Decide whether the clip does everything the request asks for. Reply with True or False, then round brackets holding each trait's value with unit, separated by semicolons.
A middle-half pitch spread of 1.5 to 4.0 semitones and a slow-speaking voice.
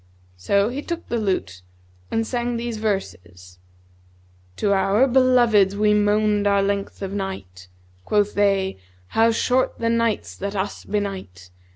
False (3.0 semitones; 145 wpm)